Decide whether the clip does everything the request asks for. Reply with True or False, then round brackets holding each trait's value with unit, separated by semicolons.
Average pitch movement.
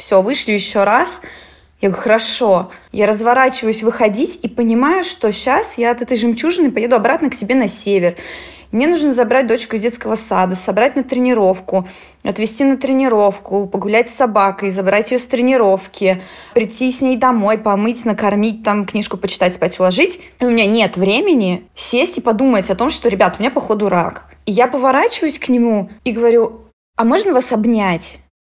True (4.1 semitones)